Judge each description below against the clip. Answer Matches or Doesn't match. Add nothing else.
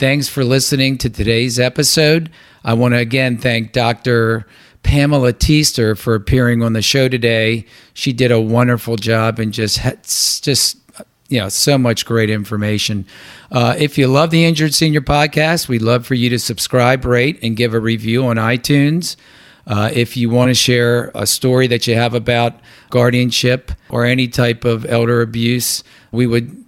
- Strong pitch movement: Doesn't match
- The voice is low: Matches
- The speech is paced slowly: Doesn't match